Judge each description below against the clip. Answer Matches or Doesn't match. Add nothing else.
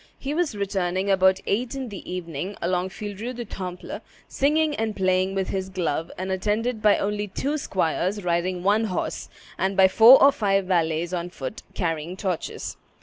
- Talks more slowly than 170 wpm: Doesn't match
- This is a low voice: Doesn't match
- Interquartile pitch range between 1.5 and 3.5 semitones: Matches